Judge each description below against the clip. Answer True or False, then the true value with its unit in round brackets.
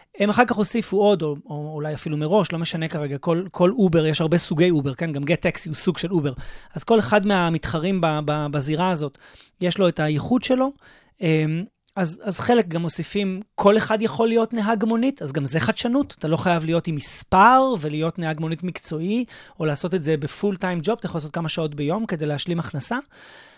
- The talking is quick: True (200 wpm)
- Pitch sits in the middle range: True (170 Hz)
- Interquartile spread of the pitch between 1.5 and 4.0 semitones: False (4.7 semitones)